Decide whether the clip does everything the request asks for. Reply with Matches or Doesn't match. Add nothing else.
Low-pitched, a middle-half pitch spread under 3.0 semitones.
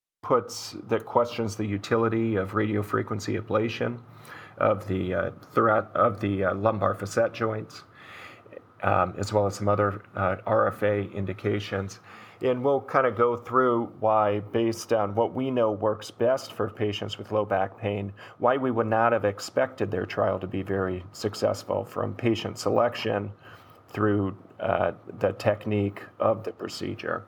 Matches